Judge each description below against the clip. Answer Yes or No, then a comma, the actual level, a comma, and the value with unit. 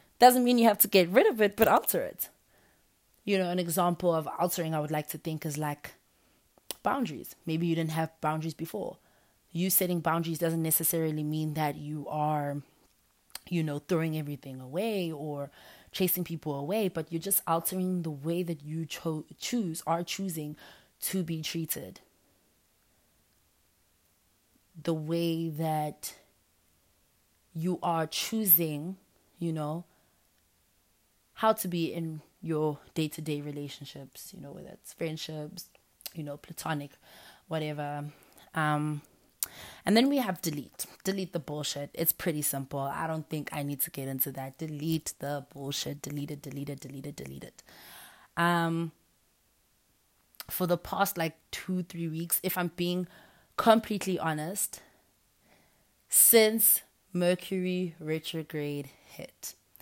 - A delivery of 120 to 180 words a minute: Yes, average, 140 wpm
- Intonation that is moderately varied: Yes, average, 3.0 semitones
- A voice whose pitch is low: No, medium, 160 Hz